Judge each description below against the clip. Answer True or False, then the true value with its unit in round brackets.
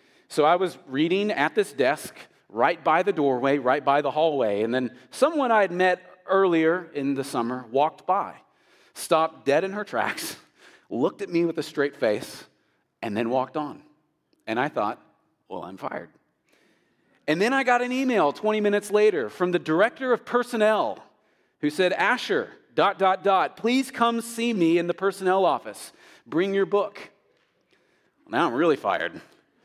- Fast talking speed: False (170 wpm)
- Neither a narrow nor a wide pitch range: False (5.7 semitones)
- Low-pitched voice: False (185 Hz)